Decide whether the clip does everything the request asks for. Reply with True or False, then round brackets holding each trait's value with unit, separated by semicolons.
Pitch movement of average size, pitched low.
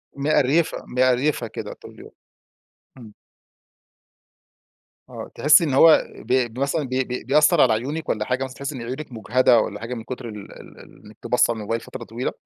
True (3.4 semitones; 130 Hz)